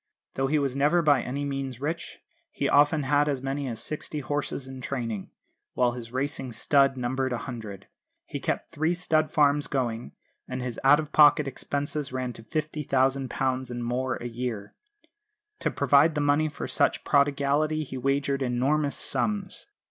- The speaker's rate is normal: Yes, average, 165 wpm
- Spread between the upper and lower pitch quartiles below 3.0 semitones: Yes, narrow, 2.5 semitones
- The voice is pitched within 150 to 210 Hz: No, medium, 140 Hz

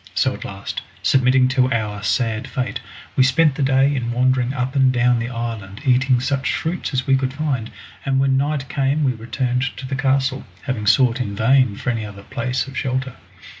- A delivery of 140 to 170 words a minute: No, average, 200 wpm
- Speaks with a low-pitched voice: Yes, low, 130 Hz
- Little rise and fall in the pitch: Yes, narrow, 2.1 semitones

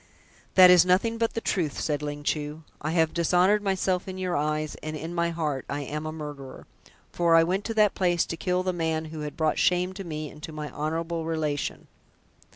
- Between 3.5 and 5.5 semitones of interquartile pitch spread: No, average, 3.0 semitones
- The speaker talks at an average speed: No, fast, 215 wpm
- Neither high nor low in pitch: Yes, medium, 165 Hz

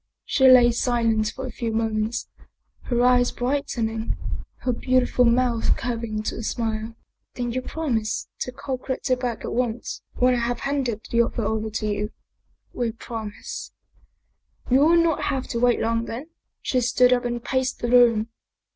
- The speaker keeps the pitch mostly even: Yes, narrow, 2.0 semitones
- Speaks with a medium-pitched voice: No, high, 240 Hz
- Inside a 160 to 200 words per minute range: Yes, average, 180 wpm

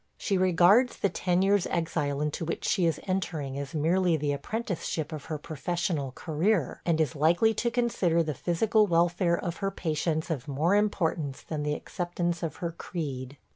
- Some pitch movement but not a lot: Yes, average, 3.5 semitones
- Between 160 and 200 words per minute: Yes, average, 175 wpm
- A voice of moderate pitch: Yes, medium, 170 Hz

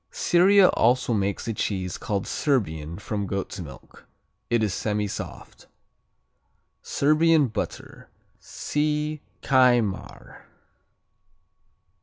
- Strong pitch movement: Yes, wide, 7.1 semitones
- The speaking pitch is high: No, low, 115 Hz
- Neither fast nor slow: No, slow, 85 wpm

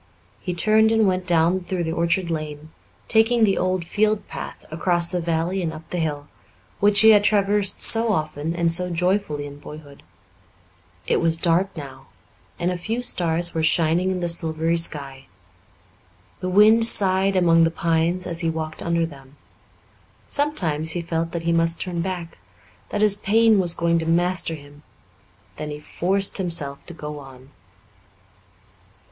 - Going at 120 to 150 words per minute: No, average, 165 wpm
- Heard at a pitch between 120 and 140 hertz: No, medium, 170 Hz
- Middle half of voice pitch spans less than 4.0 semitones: Yes, average, 2.8 semitones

